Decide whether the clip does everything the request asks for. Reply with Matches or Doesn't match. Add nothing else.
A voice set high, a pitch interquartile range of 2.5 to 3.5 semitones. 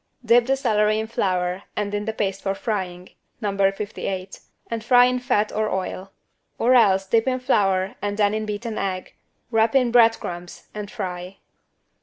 Matches